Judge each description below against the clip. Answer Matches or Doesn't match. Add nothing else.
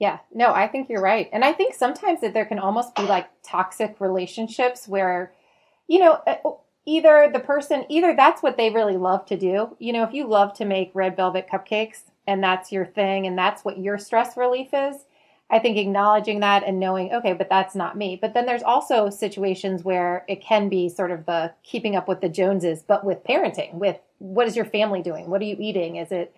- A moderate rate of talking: Doesn't match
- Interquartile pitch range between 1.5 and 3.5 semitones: Doesn't match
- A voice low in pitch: Doesn't match